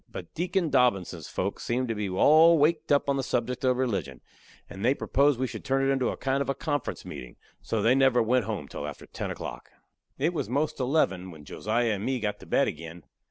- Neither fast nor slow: No, fast, 225 wpm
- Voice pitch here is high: No, low, 125 Hz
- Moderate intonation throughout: Yes, average, 4.9 semitones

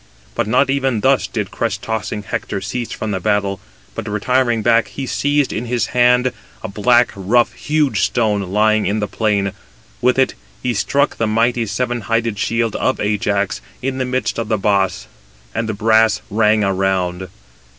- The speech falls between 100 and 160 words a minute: No, average, 170 wpm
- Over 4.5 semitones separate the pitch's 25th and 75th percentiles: No, average, 3.1 semitones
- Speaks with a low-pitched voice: Yes, low, 110 Hz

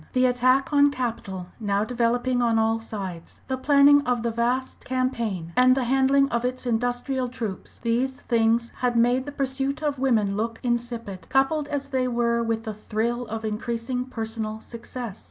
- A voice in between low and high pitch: No, high, 240 Hz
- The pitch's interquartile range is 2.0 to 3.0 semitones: Yes, narrow, 2.5 semitones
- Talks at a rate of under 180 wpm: Yes, average, 170 wpm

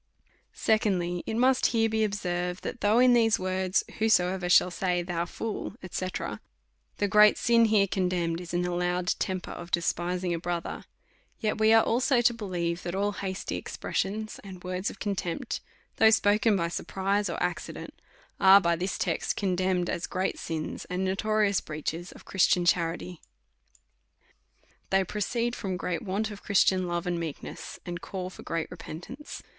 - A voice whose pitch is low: No, medium, 185 Hz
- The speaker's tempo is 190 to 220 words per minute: No, average, 165 wpm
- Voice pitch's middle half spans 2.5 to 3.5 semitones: Yes, average, 3.1 semitones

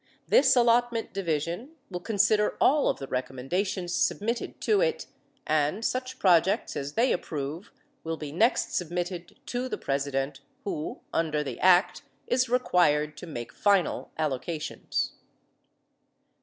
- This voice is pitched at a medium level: Yes, medium, 180 Hz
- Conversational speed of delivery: No, slow, 130 wpm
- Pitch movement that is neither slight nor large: No, wide, 7.2 semitones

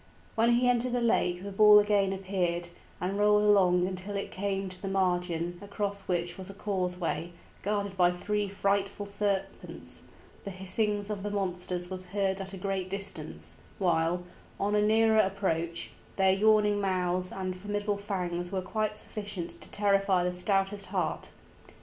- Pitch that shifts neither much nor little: No, narrow, 2.2 semitones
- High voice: Yes, high, 195 Hz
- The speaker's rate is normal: Yes, average, 160 wpm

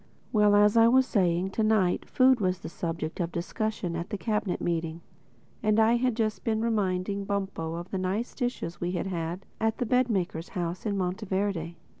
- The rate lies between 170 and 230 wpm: Yes, average, 190 wpm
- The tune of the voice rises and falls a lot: No, average, 3.9 semitones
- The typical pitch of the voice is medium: No, high, 195 Hz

